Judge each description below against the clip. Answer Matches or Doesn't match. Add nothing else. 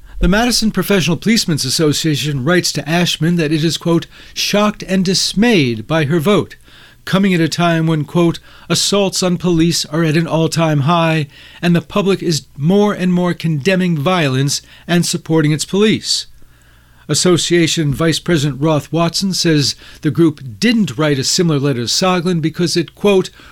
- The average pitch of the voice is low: Doesn't match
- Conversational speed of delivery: Matches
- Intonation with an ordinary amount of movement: Matches